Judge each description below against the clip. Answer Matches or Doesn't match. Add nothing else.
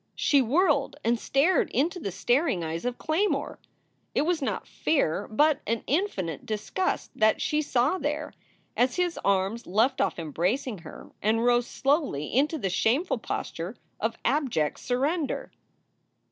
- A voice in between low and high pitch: Doesn't match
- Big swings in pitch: Matches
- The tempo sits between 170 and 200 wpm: Doesn't match